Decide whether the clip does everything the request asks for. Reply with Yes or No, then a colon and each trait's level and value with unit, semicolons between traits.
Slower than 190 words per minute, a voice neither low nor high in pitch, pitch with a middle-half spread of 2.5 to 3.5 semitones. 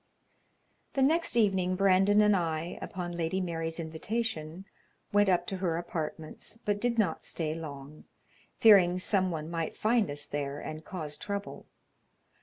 No: average, 145 wpm; medium, 180 Hz; average, 4.1 semitones